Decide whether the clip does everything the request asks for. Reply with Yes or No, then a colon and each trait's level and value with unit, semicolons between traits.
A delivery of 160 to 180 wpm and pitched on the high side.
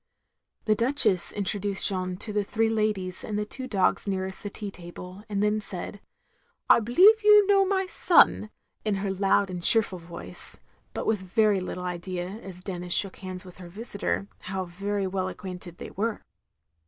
Yes: average, 175 wpm; high, 195 Hz